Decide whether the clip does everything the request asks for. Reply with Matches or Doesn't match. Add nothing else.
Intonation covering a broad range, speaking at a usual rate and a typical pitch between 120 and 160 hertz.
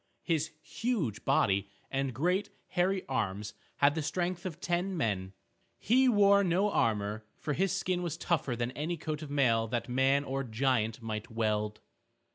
Matches